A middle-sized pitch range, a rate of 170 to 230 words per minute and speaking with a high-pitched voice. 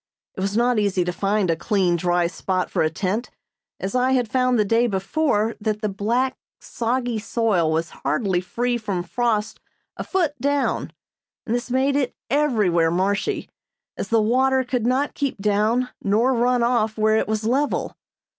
Yes: average, 4.2 semitones; average, 175 wpm; high, 220 Hz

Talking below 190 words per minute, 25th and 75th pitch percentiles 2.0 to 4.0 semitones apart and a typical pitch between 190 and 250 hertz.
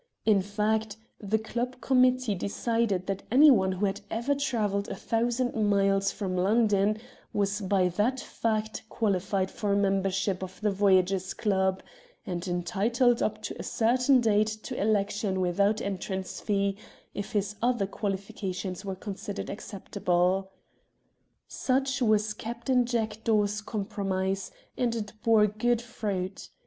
Yes: slow, 135 wpm; average, 2.7 semitones; high, 205 Hz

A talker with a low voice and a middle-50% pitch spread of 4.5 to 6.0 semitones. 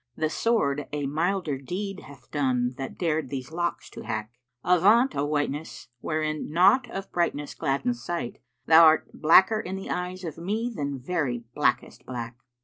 No: medium, 155 Hz; average, 4.9 semitones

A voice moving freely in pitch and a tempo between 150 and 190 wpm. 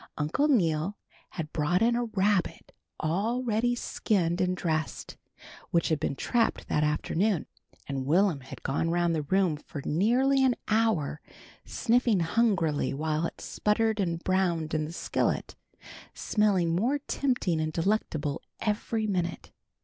No: wide, 5.8 semitones; average, 140 wpm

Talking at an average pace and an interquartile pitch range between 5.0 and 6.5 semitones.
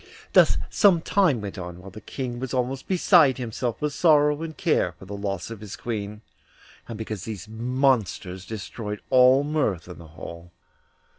Yes: average, 170 wpm; wide, 5.4 semitones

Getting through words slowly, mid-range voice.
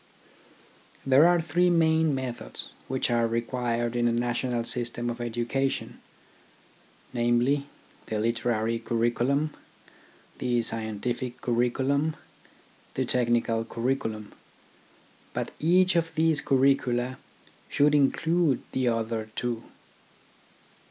No: slow, 100 wpm; low, 125 Hz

